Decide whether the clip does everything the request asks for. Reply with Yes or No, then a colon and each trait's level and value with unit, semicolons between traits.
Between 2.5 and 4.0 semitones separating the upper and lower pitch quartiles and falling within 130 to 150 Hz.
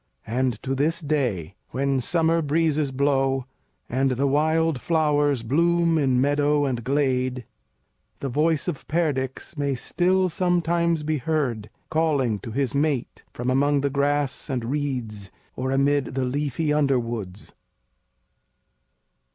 Yes: average, 3.2 semitones; medium, 140 Hz